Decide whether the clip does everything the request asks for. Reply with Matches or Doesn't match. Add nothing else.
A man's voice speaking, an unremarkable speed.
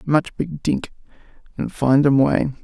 Matches